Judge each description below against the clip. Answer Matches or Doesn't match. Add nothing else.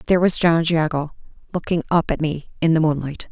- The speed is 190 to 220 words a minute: Matches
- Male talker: Doesn't match